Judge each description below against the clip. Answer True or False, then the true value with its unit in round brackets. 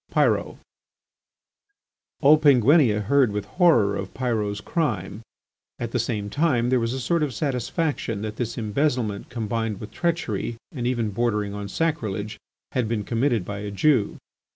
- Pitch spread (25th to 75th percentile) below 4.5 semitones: False (4.8 semitones)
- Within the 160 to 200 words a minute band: False (150 wpm)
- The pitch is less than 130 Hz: True (115 Hz)